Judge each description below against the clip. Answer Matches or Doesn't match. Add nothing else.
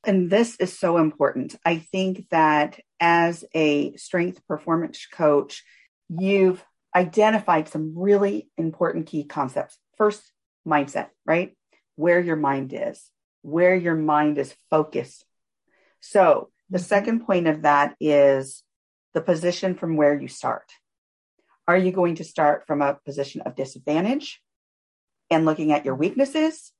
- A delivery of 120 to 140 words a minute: Matches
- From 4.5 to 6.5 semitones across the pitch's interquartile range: Doesn't match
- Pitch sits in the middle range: Matches